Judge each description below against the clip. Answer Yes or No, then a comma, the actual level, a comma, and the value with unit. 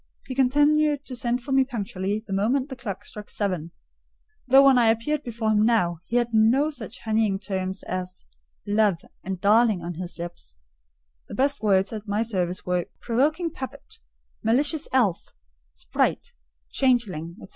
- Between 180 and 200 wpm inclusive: No, average, 160 wpm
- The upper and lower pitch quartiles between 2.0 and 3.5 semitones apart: No, average, 5.3 semitones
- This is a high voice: Yes, high, 225 Hz